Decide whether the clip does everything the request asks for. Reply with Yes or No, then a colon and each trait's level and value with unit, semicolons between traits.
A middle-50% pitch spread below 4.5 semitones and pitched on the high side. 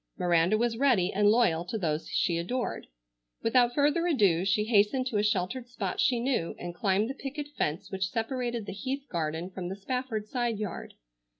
No: average, 5.2 semitones; high, 215 Hz